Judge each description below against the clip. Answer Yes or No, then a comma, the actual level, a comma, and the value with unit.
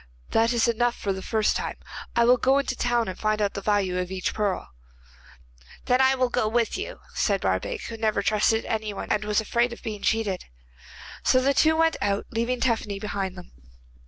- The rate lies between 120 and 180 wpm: No, fast, 205 wpm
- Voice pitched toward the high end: Yes, high, 225 Hz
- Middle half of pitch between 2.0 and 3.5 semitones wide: Yes, average, 3.0 semitones